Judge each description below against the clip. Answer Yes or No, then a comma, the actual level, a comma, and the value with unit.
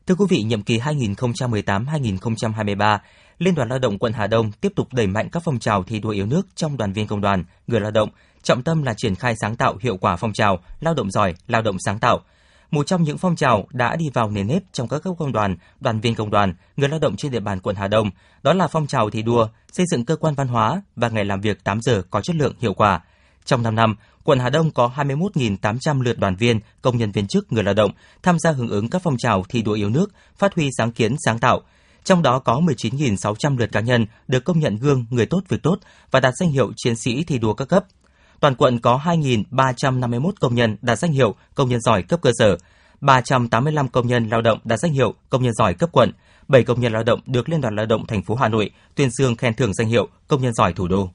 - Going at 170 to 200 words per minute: No, fast, 250 wpm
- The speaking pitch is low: Yes, low, 120 Hz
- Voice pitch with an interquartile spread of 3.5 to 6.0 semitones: Yes, average, 4.9 semitones